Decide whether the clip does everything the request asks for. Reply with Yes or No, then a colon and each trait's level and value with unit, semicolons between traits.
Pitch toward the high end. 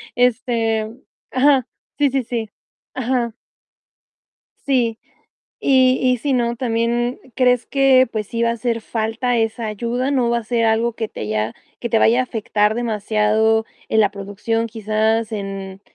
Yes: high, 230 Hz